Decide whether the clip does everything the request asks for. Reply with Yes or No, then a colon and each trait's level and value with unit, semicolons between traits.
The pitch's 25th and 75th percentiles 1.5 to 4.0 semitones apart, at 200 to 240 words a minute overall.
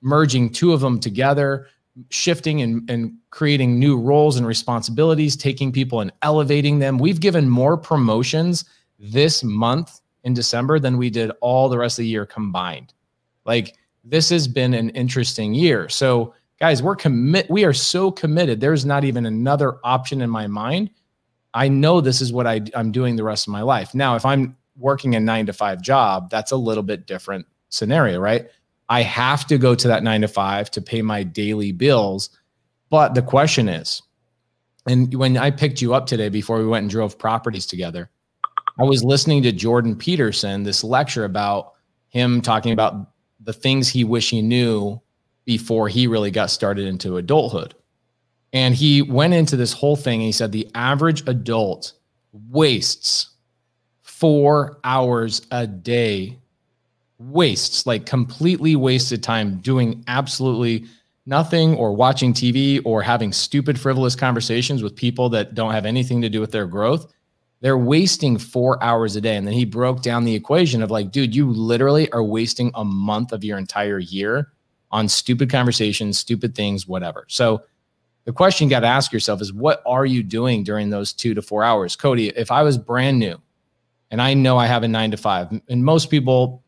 No: average, 3.7 semitones; average, 180 wpm